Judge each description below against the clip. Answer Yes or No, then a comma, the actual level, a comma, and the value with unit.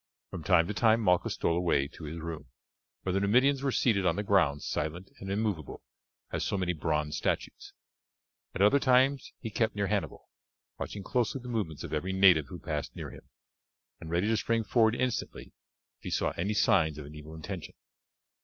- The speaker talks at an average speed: Yes, average, 190 wpm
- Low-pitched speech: Yes, very low, 95 Hz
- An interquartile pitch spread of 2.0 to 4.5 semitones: No, wide, 5.4 semitones